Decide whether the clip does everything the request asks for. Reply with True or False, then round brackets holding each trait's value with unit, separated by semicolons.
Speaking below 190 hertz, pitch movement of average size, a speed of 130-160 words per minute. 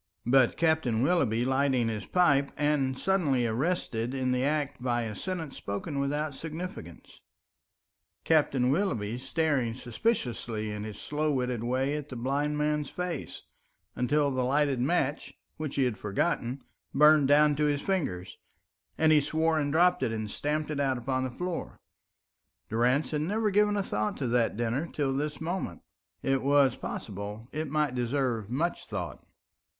True (140 Hz; 4.0 semitones; 155 wpm)